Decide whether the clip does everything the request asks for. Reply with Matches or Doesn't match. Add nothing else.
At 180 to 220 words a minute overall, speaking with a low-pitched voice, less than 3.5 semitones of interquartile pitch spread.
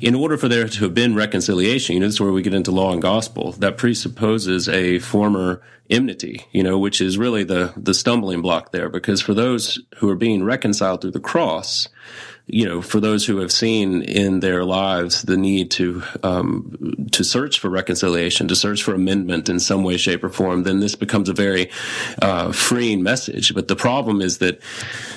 Matches